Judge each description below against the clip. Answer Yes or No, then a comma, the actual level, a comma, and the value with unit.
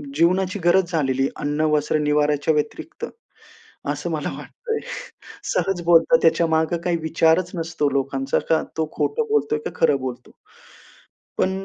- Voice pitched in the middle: Yes, medium, 160 Hz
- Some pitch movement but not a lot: Yes, average, 3.2 semitones